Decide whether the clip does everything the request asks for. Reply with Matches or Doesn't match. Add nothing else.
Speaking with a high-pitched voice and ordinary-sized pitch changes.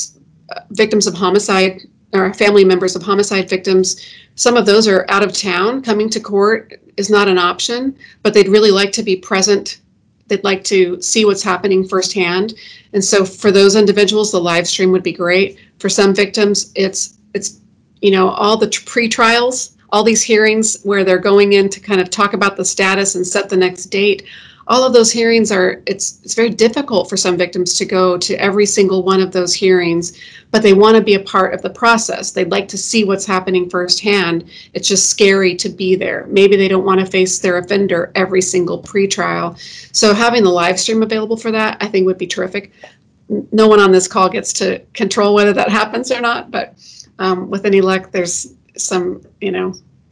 Doesn't match